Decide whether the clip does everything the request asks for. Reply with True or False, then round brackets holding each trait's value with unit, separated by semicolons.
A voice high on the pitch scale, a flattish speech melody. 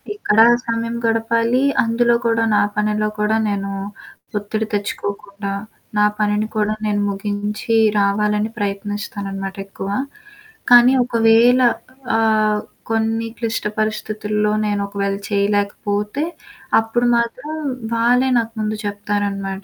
True (210 Hz; 1.9 semitones)